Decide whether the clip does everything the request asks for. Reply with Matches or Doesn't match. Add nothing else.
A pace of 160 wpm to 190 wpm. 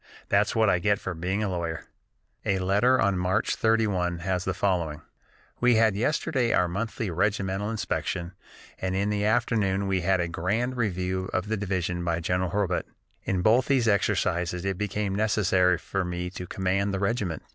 Matches